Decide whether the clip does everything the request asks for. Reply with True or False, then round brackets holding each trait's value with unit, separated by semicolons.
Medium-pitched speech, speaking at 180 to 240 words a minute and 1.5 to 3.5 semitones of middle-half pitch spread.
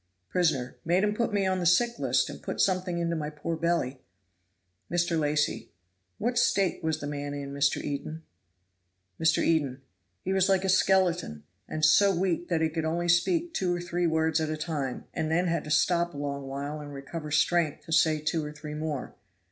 True (160 Hz; 200 wpm; 2.9 semitones)